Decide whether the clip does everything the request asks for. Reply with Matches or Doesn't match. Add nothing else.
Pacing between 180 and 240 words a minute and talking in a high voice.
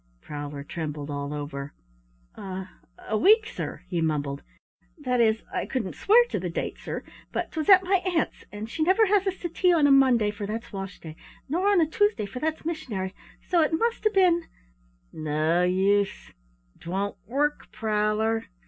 Matches